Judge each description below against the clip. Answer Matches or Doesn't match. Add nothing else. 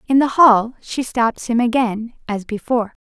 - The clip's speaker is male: Doesn't match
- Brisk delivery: Doesn't match